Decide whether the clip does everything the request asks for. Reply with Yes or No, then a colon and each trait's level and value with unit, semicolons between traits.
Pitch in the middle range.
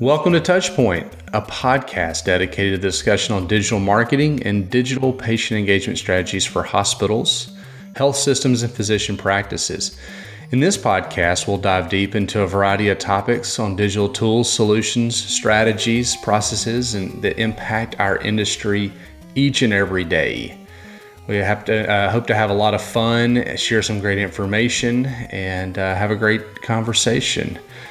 No: low, 105 Hz